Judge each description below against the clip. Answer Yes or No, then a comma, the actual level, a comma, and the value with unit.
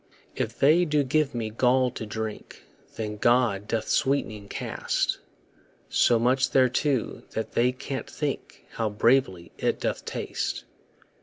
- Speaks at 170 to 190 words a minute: No, slow, 135 wpm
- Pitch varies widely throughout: No, average, 3.4 semitones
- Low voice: Yes, low, 125 Hz